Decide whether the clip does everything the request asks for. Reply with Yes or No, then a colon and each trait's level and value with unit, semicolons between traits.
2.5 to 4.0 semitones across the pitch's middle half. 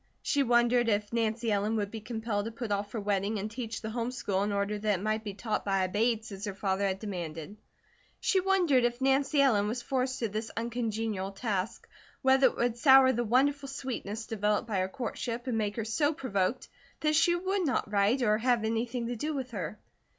Yes: average, 3.6 semitones